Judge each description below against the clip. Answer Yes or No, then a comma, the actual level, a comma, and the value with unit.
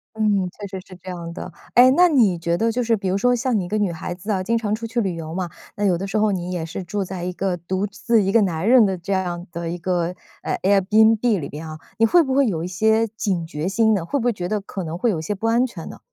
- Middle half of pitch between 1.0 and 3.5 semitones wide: No, average, 4.0 semitones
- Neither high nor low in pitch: No, high, 195 Hz